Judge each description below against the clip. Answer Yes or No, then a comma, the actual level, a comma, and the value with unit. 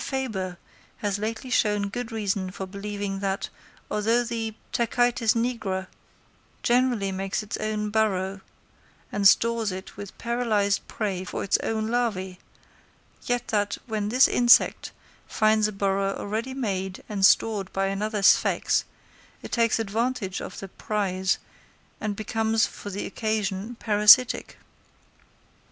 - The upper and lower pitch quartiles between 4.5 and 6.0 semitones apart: No, narrow, 2.6 semitones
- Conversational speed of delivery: No, slow, 130 wpm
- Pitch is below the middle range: No, high, 210 Hz